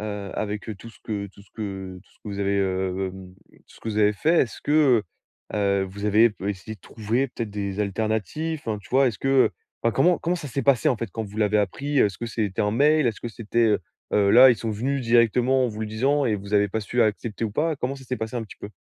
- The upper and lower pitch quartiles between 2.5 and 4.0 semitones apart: Yes, average, 3.7 semitones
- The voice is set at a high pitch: No, low, 110 Hz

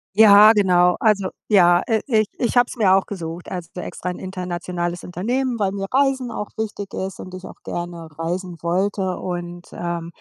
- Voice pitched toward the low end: No, medium, 185 Hz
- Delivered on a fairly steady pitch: No, average, 3.1 semitones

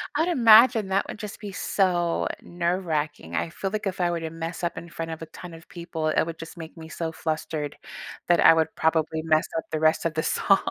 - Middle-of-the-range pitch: Yes, medium, 165 Hz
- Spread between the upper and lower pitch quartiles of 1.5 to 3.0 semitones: Yes, average, 2.7 semitones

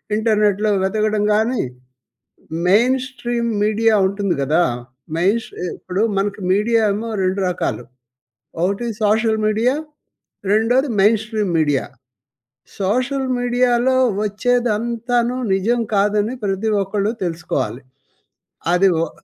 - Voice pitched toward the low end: No, high, 215 Hz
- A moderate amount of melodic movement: Yes, average, 3.2 semitones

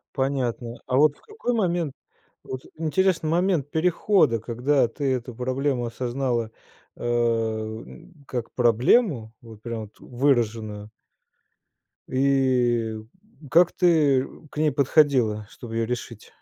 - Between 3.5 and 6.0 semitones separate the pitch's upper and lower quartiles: Yes, average, 4.6 semitones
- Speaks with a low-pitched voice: Yes, low, 130 Hz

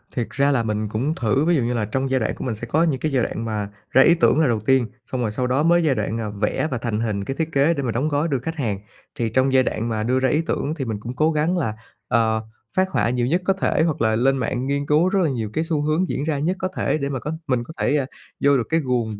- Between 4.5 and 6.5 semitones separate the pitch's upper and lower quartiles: Yes, average, 5.0 semitones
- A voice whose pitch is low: Yes, low, 130 Hz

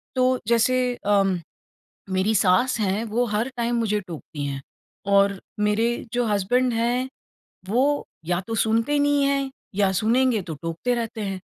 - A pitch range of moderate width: Yes, average, 3.8 semitones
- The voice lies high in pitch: Yes, high, 225 Hz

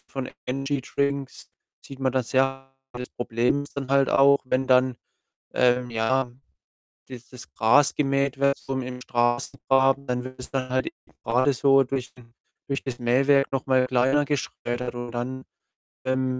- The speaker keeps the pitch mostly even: Yes, narrow, 1.6 semitones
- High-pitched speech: No, low, 130 Hz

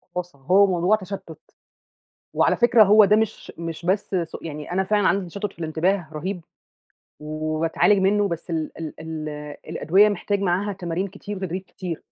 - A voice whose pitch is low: No, medium, 185 Hz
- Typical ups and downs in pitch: Yes, average, 3.5 semitones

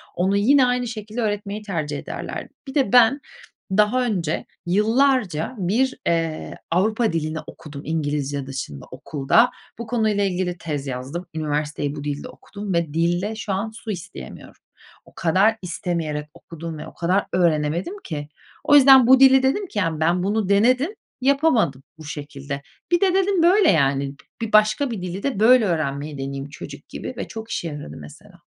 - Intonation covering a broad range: Yes, wide, 7.1 semitones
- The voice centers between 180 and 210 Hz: Yes, medium, 185 Hz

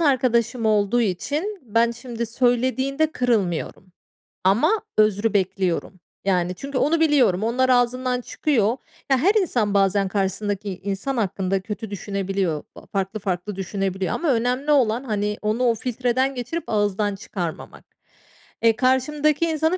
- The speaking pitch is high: Yes, high, 225 Hz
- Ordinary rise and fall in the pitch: Yes, average, 4.7 semitones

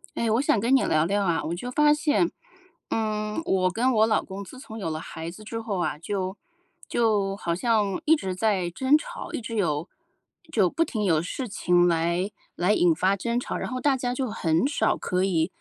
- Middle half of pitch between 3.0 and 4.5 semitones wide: No, average, 5.0 semitones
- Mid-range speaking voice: No, high, 205 Hz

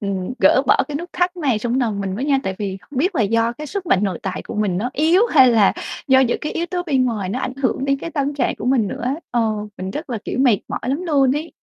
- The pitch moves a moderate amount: No, wide, 5.7 semitones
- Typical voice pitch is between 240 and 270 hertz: Yes, very high, 255 Hz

